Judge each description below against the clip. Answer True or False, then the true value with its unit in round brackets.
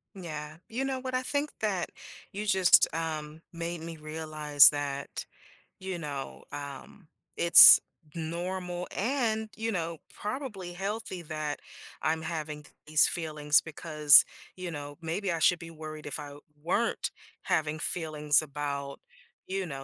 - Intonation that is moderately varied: True (3.8 semitones)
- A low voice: False (160 Hz)